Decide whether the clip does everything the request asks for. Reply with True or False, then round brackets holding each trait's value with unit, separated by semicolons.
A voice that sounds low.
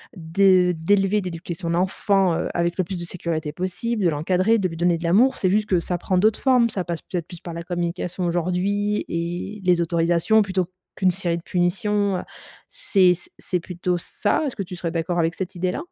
False (180 Hz)